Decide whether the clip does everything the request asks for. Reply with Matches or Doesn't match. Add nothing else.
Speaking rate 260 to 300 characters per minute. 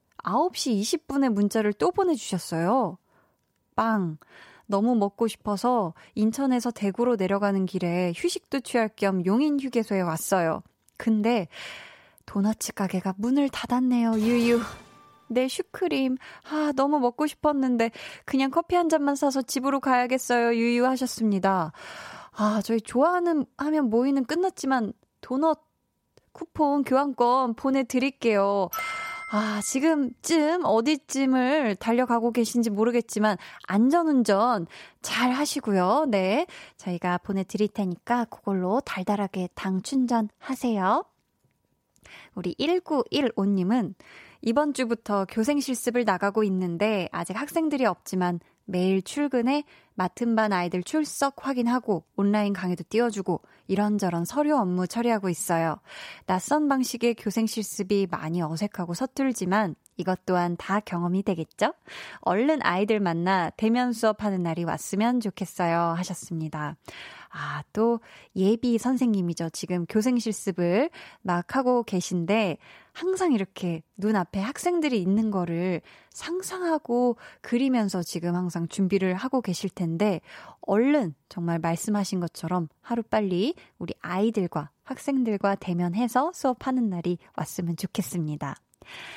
Matches